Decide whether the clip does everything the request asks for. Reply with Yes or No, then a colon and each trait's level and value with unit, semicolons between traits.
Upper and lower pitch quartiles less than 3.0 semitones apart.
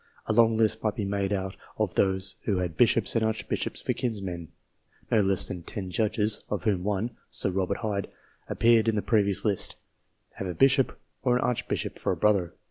Yes: narrow, 2.6 semitones